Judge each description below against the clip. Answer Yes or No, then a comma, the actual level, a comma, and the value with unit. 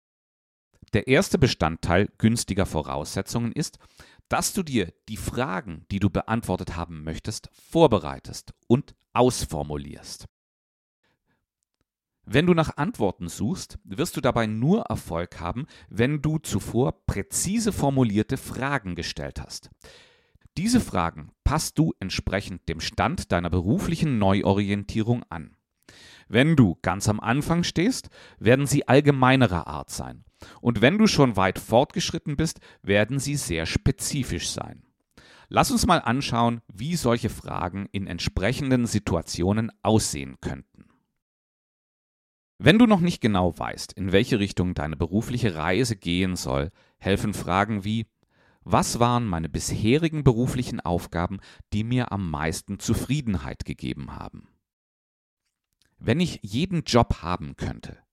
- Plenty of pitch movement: Yes, wide, 6.6 semitones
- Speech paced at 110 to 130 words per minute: Yes, slow, 125 wpm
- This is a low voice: Yes, low, 105 Hz